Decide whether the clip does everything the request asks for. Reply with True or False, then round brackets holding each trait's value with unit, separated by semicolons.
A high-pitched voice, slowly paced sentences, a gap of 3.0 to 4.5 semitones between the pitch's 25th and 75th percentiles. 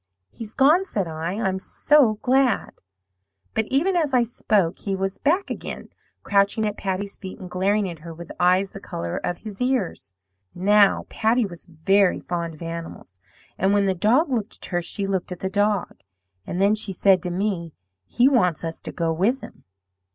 False (195 Hz; 190 wpm; 3.8 semitones)